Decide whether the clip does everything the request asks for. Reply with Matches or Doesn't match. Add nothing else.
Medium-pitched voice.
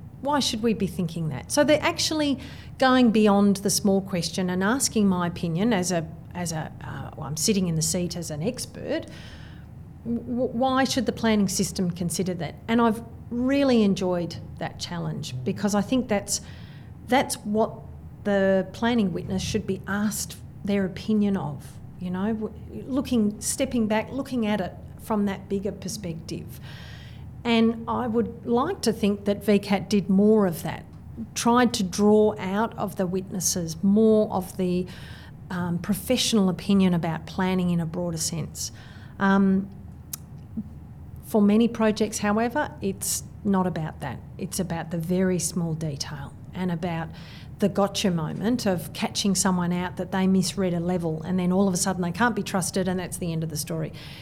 Doesn't match